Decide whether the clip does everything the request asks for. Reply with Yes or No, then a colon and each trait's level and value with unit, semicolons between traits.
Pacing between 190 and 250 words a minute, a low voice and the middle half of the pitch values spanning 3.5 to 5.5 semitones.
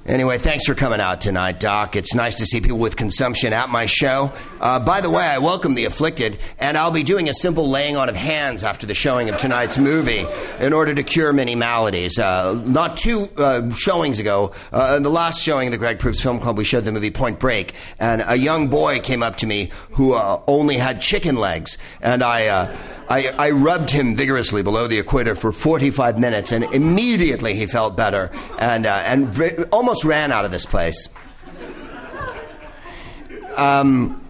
Yes: average, 200 wpm; low, 130 Hz; average, 4.1 semitones